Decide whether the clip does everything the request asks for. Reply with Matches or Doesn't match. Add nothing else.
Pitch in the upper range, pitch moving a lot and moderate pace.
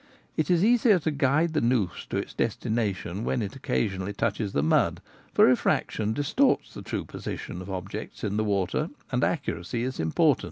Doesn't match